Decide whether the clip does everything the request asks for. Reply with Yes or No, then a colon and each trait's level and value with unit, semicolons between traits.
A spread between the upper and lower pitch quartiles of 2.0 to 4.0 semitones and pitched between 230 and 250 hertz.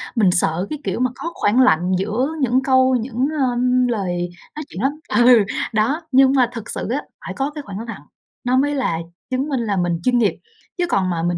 No: average, 5.2 semitones; high, 240 Hz